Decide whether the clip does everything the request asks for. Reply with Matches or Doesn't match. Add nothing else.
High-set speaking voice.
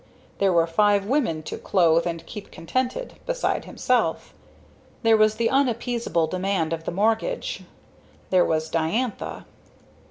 Matches